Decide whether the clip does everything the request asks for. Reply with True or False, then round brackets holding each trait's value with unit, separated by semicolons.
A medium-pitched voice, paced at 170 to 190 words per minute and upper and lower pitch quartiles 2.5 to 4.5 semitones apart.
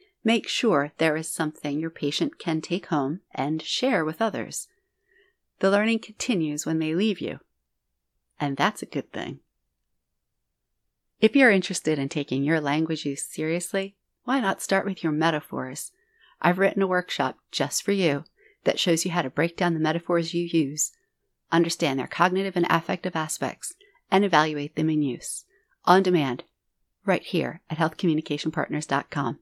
False (165 Hz; 155 wpm; 4.2 semitones)